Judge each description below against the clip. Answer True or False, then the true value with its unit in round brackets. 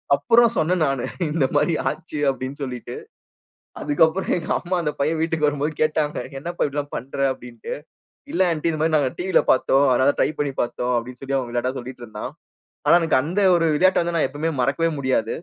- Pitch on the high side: False (145 Hz)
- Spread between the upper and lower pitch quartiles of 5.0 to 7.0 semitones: False (3.8 semitones)